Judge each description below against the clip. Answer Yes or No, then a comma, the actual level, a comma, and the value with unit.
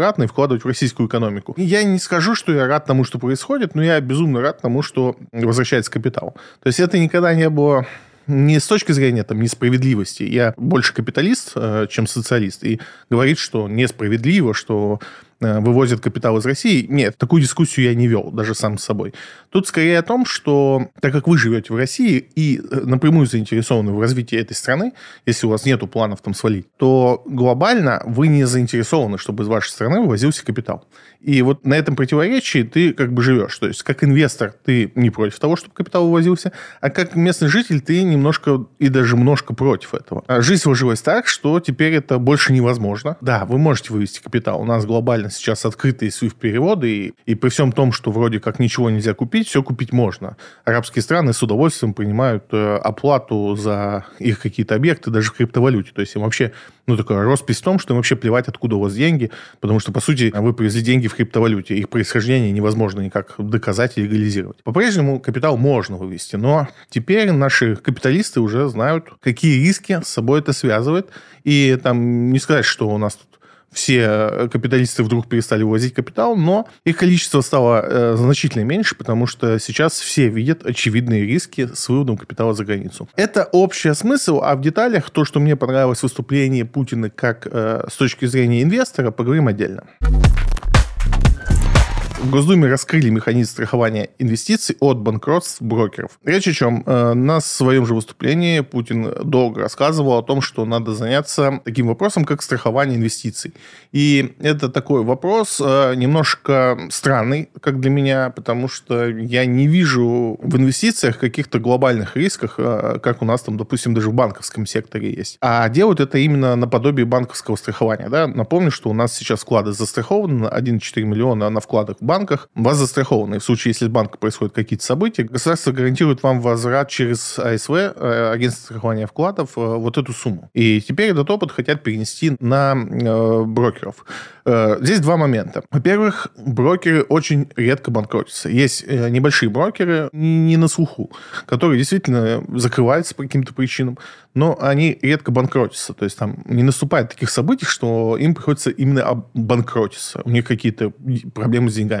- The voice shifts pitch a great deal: No, average, 4.4 semitones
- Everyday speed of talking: No, fast, 170 wpm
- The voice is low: Yes, low, 125 Hz